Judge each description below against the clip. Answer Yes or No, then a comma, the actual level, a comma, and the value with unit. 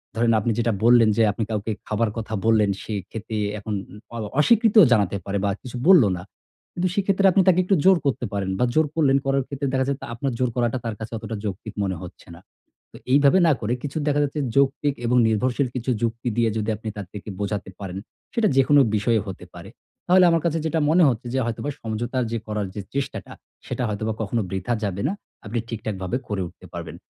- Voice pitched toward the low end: Yes, low, 120 Hz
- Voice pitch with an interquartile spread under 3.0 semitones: No, average, 4.7 semitones